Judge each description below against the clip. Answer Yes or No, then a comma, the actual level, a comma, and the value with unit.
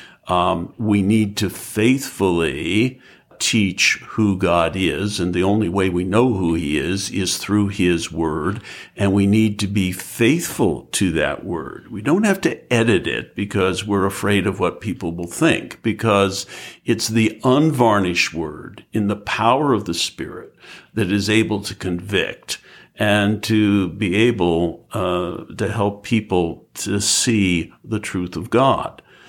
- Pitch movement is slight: No, average, 3.0 semitones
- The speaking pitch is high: No, low, 100 Hz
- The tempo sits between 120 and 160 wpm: Yes, average, 155 wpm